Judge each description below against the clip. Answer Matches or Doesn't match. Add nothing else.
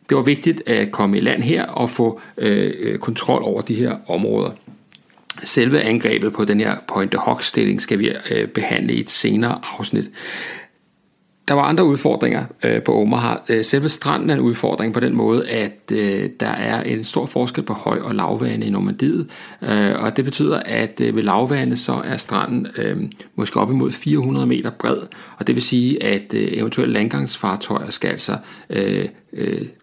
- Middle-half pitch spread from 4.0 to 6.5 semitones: Matches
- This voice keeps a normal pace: Matches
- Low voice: Matches